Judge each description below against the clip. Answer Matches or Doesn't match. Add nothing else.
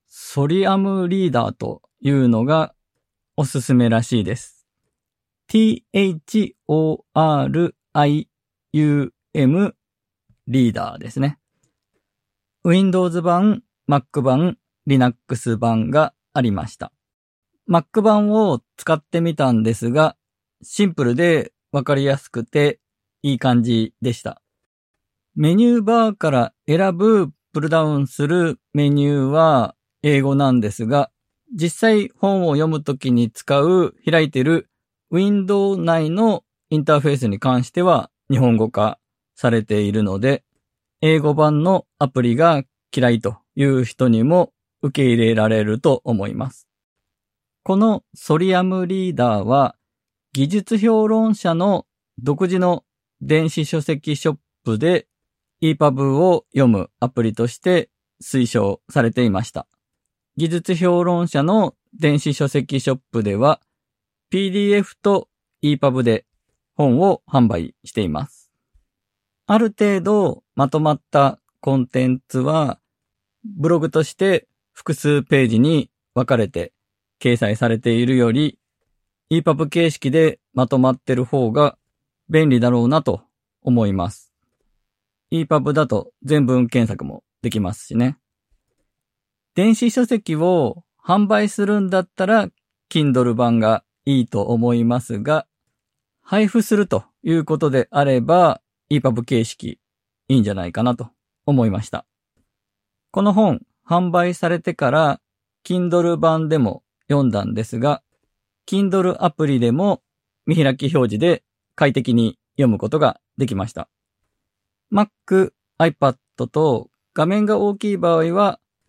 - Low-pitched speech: Doesn't match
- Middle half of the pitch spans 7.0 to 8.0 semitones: Doesn't match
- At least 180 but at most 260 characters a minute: Matches